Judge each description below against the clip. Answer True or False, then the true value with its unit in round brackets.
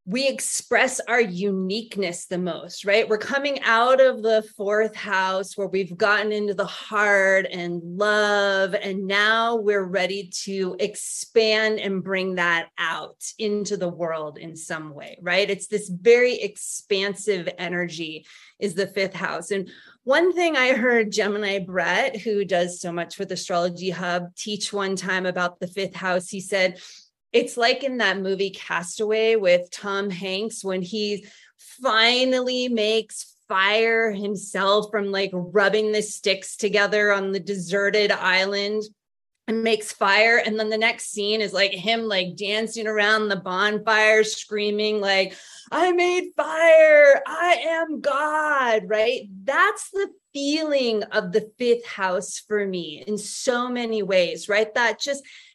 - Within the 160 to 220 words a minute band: False (150 wpm)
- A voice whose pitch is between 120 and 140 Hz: False (205 Hz)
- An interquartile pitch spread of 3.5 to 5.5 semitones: False (3.0 semitones)